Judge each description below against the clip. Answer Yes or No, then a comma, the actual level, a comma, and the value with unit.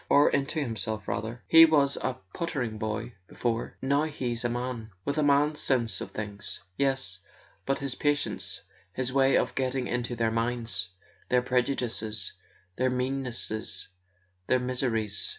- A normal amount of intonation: Yes, average, 3.3 semitones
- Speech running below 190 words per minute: Yes, average, 150 wpm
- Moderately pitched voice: No, low, 125 Hz